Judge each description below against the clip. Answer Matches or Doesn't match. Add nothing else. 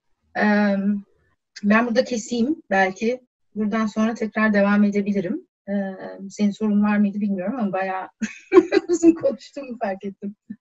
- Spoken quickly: Doesn't match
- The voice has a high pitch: Matches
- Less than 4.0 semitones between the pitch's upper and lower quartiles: Matches